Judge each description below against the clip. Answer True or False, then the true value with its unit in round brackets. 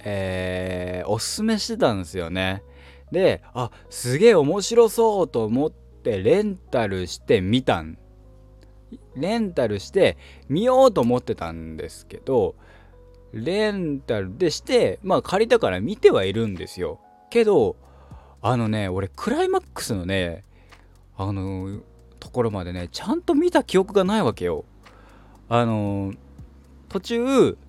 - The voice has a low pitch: True (100 Hz)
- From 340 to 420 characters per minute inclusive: False (260 characters per minute)